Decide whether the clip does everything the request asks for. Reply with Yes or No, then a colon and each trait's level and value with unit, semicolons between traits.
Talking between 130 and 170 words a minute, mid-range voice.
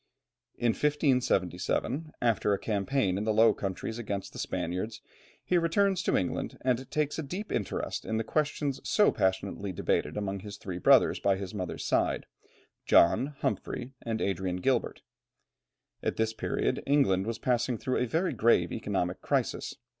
No: average, 155 wpm; low, 115 Hz